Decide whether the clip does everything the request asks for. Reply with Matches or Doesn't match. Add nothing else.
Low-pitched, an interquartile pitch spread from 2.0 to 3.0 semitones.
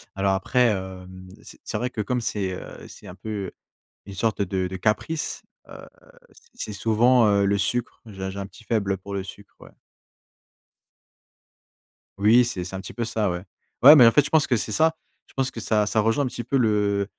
Doesn't match